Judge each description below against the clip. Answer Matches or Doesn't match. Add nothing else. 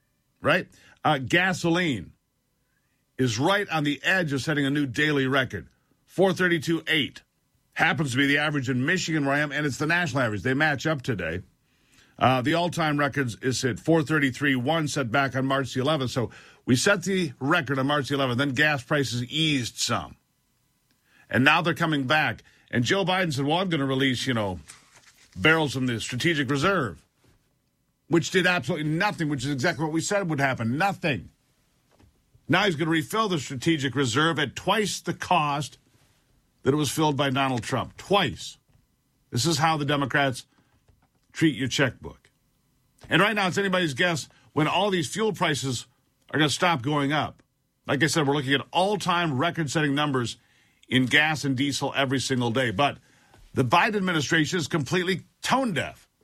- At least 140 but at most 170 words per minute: Doesn't match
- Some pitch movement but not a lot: Matches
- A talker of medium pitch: Matches